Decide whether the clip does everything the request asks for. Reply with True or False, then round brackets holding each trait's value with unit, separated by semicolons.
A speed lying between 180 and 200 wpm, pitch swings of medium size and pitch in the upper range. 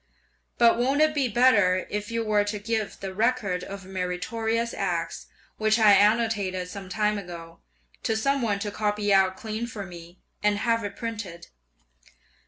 False (165 wpm; 3.1 semitones; 210 Hz)